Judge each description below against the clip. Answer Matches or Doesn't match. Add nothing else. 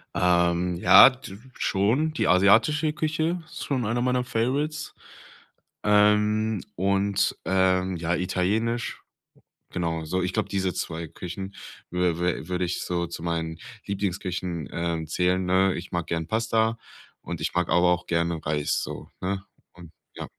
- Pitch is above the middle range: Doesn't match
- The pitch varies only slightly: Doesn't match